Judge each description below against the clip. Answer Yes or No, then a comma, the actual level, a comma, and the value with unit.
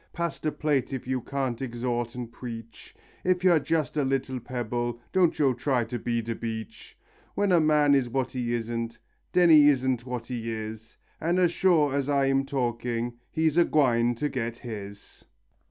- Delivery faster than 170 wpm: Yes, average, 180 wpm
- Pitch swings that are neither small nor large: Yes, average, 3.8 semitones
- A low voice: Yes, low, 125 Hz